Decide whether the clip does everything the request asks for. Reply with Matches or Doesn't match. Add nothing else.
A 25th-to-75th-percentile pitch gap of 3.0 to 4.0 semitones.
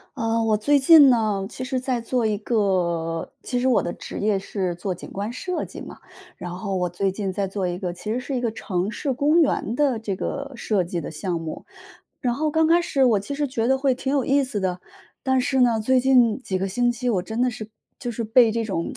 Doesn't match